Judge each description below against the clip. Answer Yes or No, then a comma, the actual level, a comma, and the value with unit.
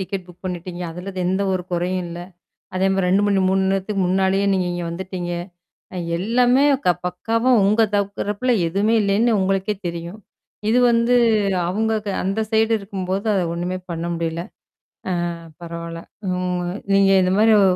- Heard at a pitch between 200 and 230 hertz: No, high, 190 Hz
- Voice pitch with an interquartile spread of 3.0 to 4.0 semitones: No, narrow, 2.5 semitones